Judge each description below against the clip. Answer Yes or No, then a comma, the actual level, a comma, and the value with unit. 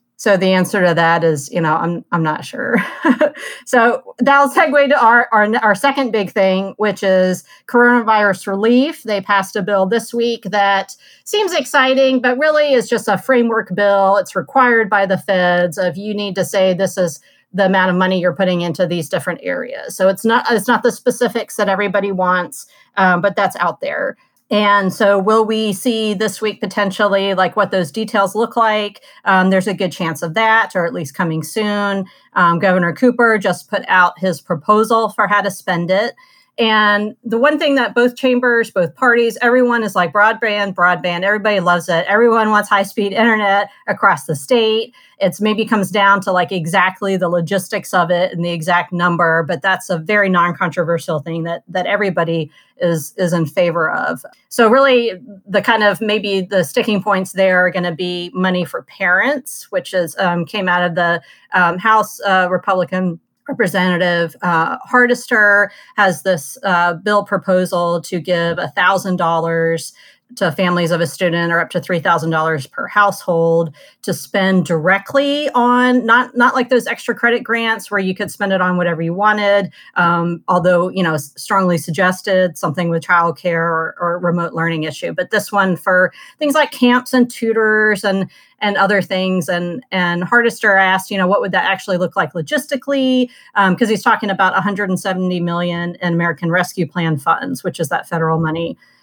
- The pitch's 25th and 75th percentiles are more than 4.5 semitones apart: No, average, 4.1 semitones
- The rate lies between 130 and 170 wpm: No, average, 185 wpm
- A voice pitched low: No, high, 195 Hz